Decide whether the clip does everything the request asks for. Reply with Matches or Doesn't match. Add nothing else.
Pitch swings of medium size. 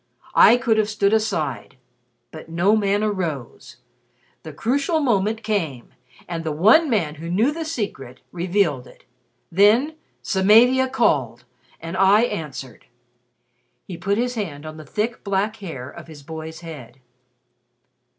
Doesn't match